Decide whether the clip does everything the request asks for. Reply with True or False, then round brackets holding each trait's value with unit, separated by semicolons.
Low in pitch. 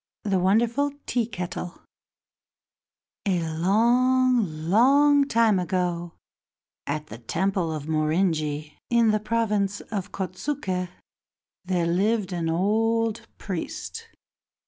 False (195 Hz)